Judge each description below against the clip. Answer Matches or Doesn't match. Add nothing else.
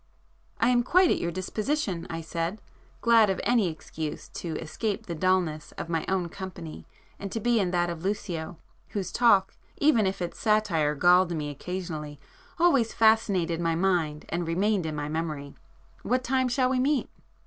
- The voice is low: Doesn't match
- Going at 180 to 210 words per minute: Doesn't match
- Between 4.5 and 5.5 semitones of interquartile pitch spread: Matches